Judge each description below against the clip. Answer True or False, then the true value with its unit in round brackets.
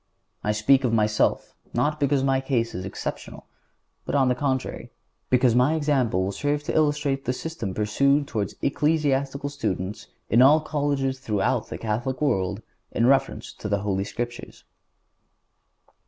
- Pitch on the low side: True (130 Hz)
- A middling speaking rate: True (150 wpm)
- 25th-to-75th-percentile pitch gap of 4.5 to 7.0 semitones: True (4.9 semitones)